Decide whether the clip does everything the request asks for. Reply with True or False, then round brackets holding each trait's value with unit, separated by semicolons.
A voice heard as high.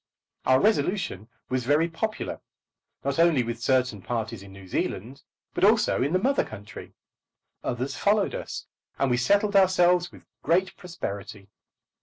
False (140 Hz)